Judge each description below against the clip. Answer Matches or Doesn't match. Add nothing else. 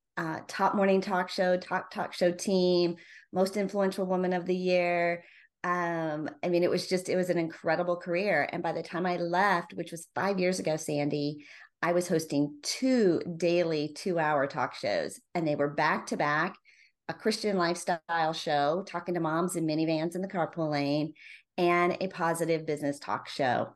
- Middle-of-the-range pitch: Matches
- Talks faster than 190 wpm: Doesn't match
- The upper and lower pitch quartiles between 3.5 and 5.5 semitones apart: Doesn't match